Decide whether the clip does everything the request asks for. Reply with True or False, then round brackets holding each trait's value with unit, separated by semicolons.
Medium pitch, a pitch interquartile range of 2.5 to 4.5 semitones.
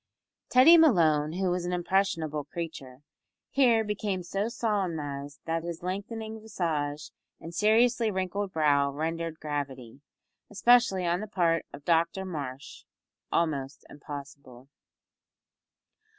False (170 Hz; 5.5 semitones)